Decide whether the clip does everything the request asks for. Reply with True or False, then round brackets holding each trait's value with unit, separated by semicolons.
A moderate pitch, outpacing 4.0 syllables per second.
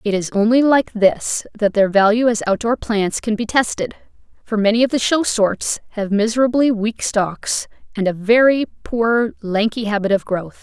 False (220 Hz; 4.5 syllables/s)